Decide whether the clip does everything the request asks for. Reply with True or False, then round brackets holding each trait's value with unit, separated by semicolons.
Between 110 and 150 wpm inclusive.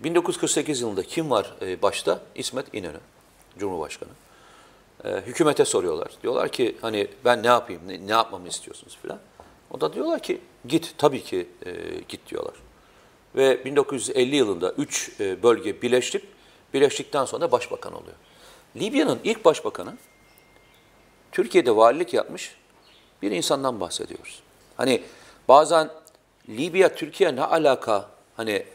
True (115 wpm)